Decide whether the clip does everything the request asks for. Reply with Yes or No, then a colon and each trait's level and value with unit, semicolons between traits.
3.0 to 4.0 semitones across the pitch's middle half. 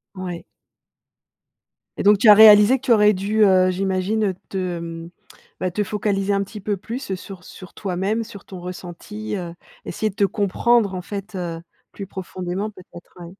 No: narrow, 2.5 semitones